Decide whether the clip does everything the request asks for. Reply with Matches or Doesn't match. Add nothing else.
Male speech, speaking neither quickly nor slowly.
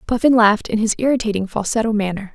Doesn't match